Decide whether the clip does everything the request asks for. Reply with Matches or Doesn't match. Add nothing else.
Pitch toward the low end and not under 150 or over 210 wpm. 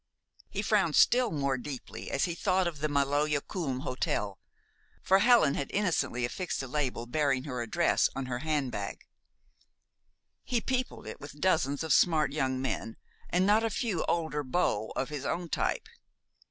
Doesn't match